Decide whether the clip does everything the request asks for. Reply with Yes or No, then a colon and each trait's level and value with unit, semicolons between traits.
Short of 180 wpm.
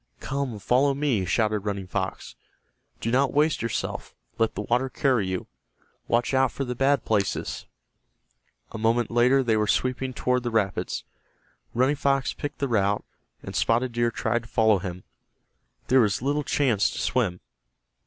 Yes: average, 160 wpm